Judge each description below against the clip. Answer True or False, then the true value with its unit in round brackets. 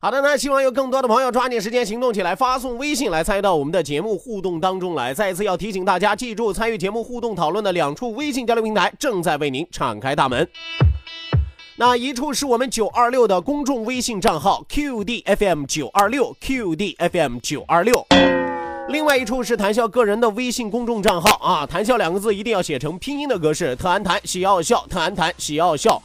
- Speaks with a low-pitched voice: False (225 Hz)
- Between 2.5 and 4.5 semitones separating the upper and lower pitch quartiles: False (5.1 semitones)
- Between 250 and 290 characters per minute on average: False (335 characters per minute)